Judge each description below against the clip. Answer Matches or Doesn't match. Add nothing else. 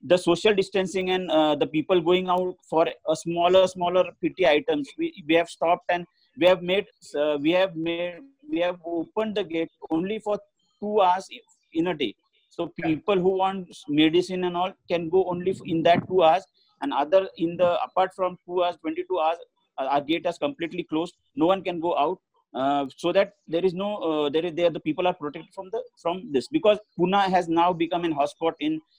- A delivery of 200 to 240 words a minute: Matches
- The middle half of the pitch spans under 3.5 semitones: Matches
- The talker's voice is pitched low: Doesn't match